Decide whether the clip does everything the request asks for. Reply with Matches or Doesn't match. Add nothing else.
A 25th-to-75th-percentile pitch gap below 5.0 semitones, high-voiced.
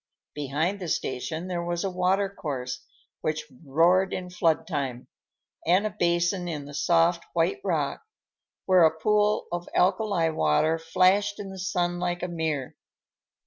Doesn't match